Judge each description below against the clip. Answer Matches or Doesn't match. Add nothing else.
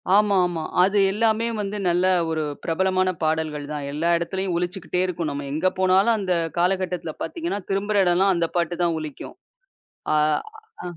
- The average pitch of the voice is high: Doesn't match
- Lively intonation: Doesn't match